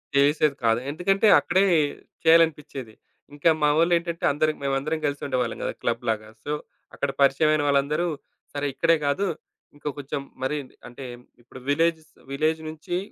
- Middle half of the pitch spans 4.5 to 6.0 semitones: No, average, 2.8 semitones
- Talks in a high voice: No, medium, 150 Hz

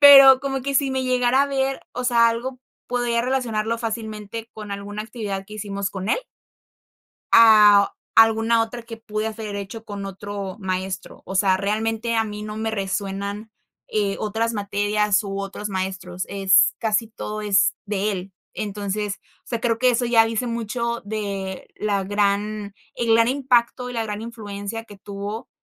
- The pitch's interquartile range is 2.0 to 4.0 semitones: Yes, narrow, 2.5 semitones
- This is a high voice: Yes, high, 215 Hz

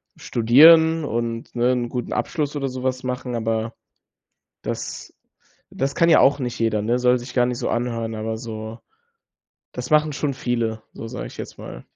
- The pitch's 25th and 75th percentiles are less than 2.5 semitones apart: No, average, 2.8 semitones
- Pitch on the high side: No, low, 125 Hz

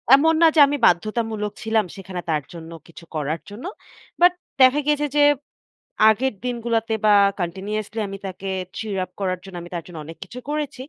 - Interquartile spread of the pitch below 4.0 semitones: No, wide, 5.4 semitones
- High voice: Yes, high, 210 Hz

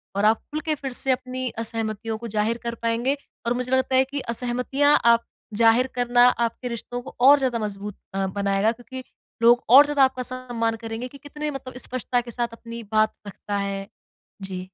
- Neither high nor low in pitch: No, high, 240 Hz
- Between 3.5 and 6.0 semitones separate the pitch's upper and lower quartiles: No, average, 2.7 semitones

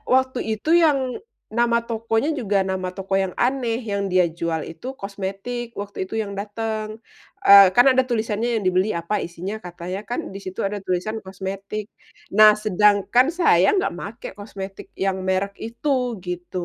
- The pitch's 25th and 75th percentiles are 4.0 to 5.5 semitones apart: No, average, 3.2 semitones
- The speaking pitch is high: Yes, high, 205 Hz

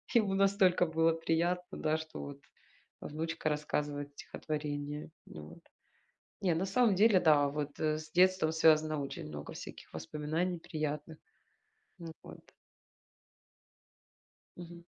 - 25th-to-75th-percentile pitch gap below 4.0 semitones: Yes, average, 2.9 semitones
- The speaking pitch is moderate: Yes, medium, 160 Hz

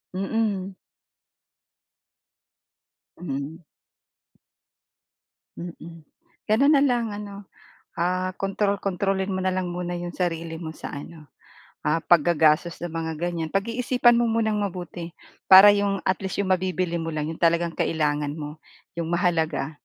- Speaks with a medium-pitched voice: Yes, medium, 175 Hz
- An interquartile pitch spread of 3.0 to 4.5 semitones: Yes, average, 3.3 semitones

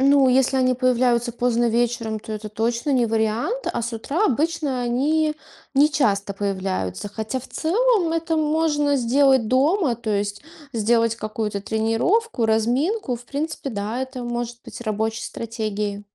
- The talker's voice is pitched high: Yes, high, 240 Hz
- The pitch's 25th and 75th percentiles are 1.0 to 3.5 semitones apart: No, average, 4.4 semitones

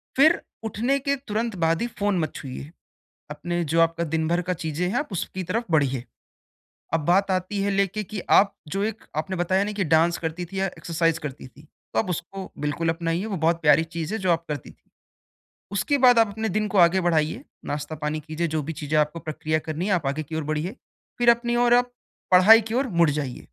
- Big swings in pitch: No, average, 4.4 semitones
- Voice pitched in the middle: Yes, medium, 175 Hz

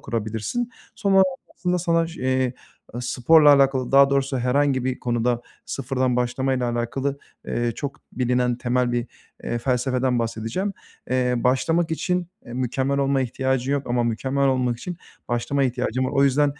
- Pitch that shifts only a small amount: Yes, narrow, 2.3 semitones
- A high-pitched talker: No, low, 130 Hz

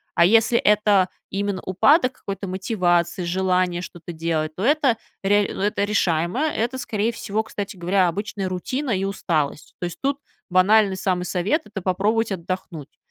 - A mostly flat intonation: No, average, 3.3 semitones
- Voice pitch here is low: No, high, 195 Hz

